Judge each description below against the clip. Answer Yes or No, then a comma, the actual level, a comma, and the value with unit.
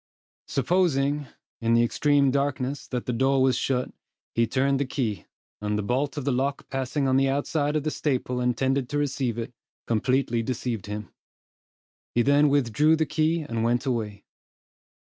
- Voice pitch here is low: Yes, low, 130 Hz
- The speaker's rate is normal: Yes, average, 165 wpm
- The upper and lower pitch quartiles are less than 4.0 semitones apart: Yes, average, 3.2 semitones